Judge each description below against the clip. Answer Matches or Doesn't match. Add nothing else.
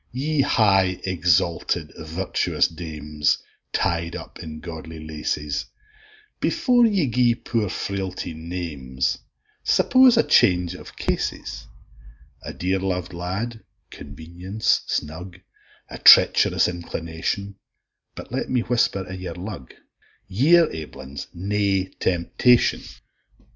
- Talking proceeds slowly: Matches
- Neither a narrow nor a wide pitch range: Matches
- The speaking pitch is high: Doesn't match